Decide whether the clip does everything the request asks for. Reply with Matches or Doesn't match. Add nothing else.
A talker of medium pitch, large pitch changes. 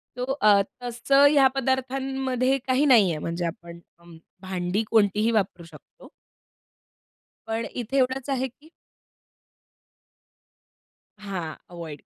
Doesn't match